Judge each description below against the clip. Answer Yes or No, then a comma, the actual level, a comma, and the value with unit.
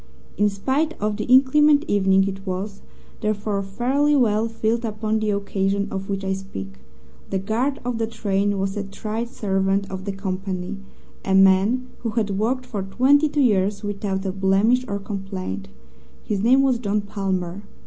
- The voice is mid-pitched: No, high, 205 Hz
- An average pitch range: Yes, average, 3.0 semitones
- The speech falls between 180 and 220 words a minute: No, average, 170 wpm